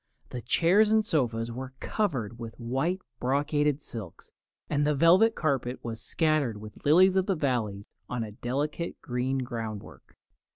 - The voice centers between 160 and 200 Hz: No, low, 135 Hz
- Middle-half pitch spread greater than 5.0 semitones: Yes, wide, 5.4 semitones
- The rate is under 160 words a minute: Yes, average, 150 wpm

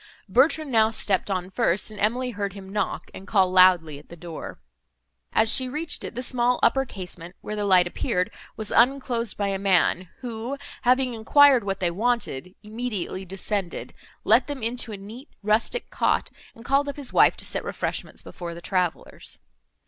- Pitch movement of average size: Yes, average, 4.8 semitones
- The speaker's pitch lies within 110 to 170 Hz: No, high, 210 Hz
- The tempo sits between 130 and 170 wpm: No, average, 180 wpm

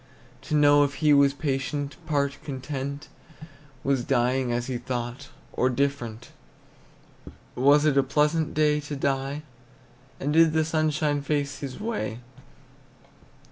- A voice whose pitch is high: No, medium, 140 Hz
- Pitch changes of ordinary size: No, narrow, 2.0 semitones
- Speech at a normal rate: No, slow, 130 wpm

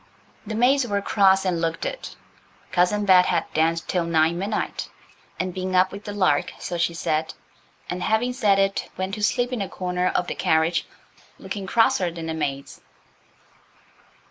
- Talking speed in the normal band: Yes, average, 170 wpm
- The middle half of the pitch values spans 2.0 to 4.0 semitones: Yes, average, 3.5 semitones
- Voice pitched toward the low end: No, medium, 185 Hz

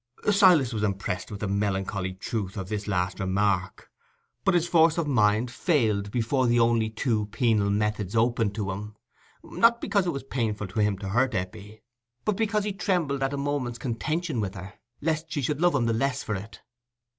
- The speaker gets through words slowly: No, average, 195 wpm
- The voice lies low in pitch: Yes, low, 115 Hz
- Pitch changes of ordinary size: No, wide, 5.9 semitones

